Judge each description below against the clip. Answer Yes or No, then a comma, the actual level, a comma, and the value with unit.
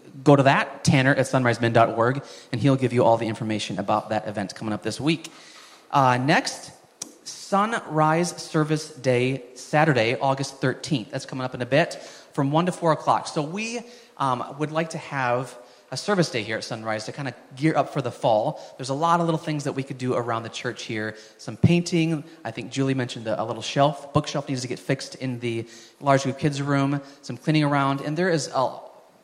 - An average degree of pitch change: Yes, average, 4.1 semitones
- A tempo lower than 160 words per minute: No, fast, 205 wpm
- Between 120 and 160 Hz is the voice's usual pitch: Yes, low, 135 Hz